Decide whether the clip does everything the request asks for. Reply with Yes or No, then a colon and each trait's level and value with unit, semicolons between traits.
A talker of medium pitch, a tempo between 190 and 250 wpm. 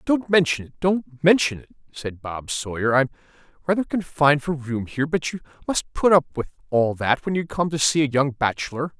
Yes: medium, 145 Hz; fast, 205 wpm